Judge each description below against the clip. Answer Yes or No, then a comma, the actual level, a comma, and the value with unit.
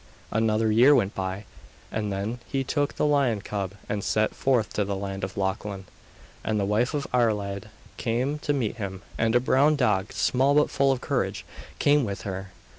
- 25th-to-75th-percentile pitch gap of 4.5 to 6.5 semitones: Yes, average, 4.8 semitones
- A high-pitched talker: No, low, 110 Hz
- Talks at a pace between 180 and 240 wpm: Yes, average, 190 wpm